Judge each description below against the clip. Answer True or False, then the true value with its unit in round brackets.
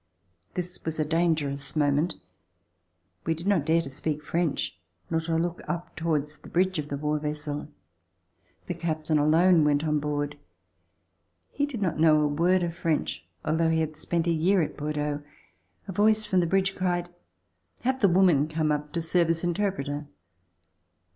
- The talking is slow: False (170 wpm)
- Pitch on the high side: False (160 Hz)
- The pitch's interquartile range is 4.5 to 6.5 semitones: False (2.8 semitones)